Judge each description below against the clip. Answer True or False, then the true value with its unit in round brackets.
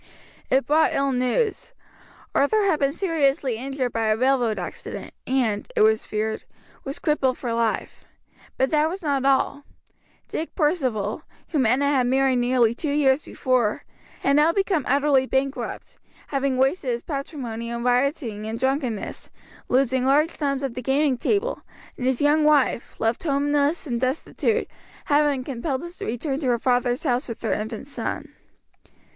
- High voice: True (270 Hz)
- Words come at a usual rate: True (160 wpm)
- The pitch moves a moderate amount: True (3.1 semitones)